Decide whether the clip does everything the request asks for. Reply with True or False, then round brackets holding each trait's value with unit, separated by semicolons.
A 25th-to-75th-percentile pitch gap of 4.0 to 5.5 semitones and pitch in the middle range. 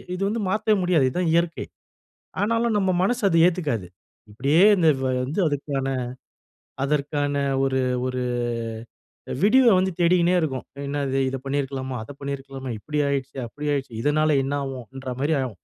True (4.6 semitones; 145 Hz)